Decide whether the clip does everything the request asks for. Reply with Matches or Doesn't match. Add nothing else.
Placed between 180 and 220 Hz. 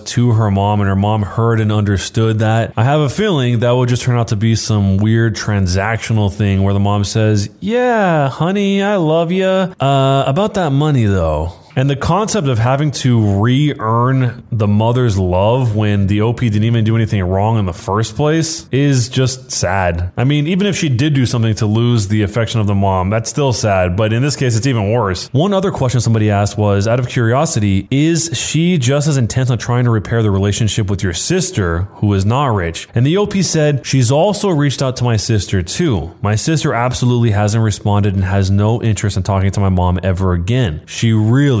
Doesn't match